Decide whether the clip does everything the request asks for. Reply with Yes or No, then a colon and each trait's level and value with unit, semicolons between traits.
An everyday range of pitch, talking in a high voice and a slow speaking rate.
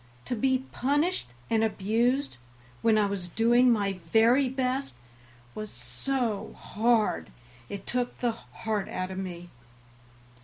Yes: average, 4.1 semitones; high, 225 Hz; slow, 125 wpm